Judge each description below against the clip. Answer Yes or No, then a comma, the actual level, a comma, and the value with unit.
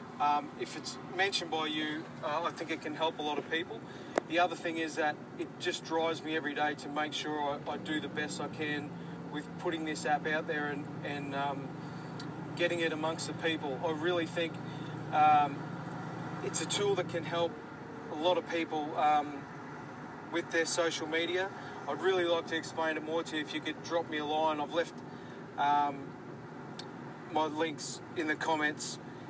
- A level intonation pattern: Yes, narrow, 1.6 semitones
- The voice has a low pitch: No, medium, 155 Hz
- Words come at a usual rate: Yes, average, 195 wpm